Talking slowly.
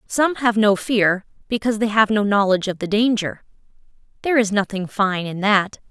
No: average, 185 wpm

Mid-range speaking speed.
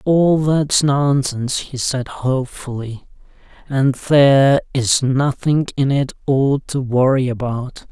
No: slow, 120 wpm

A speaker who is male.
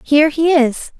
No: female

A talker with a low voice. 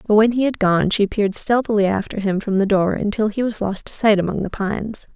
No: high, 210 Hz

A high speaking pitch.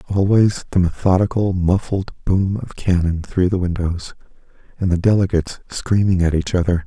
No: very low, 90 Hz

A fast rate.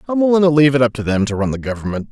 Yes: fast, 340 wpm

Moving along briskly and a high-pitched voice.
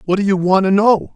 Yes: fast, 315 wpm; high, 195 Hz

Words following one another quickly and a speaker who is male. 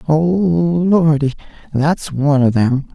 No: slow, 120 wpm; male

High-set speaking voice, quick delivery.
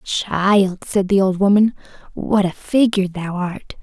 No: high, 195 Hz; average, 155 wpm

